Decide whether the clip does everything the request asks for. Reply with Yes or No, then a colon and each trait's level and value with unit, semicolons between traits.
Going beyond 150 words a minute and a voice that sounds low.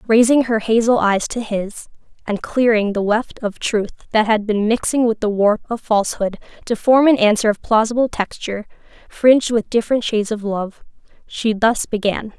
No: average, 180 wpm; high, 220 Hz